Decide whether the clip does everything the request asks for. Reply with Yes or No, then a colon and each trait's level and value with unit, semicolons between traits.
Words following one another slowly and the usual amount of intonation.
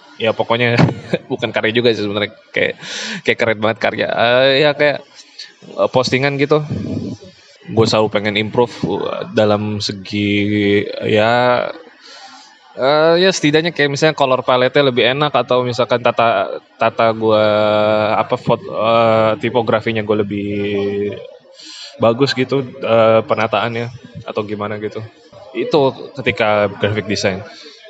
No: average, 120 wpm; average, 3.3 semitones